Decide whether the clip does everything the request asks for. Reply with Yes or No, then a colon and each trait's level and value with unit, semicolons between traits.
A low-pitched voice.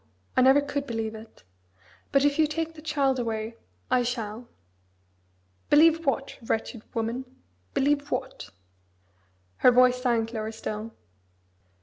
No: very high, 250 Hz